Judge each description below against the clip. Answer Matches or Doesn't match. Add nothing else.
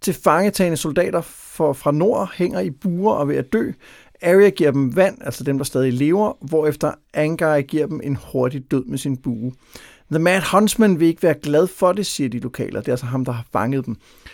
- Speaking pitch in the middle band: Matches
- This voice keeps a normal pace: Matches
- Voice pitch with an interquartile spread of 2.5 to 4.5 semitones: Doesn't match